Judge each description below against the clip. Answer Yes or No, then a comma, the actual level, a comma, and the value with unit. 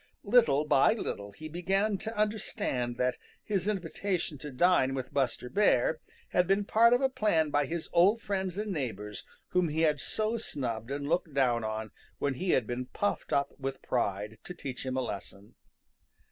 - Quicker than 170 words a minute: Yes, average, 180 wpm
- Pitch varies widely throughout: Yes, wide, 7.4 semitones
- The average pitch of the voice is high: No, medium, 150 Hz